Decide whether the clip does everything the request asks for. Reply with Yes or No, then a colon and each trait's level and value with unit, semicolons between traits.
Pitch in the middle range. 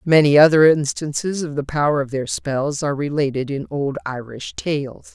Yes: medium, 145 Hz